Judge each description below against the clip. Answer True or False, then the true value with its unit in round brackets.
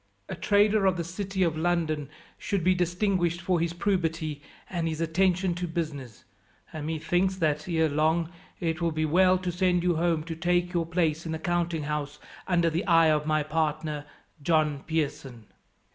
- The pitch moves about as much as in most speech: False (2.2 semitones)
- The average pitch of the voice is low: False (165 Hz)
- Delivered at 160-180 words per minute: True (175 wpm)